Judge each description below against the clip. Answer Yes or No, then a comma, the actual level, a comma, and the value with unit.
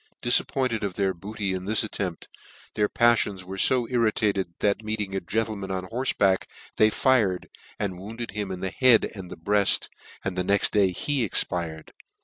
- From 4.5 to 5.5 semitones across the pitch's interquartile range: No, average, 2.9 semitones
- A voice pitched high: No, low, 100 Hz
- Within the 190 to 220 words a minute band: No, average, 170 wpm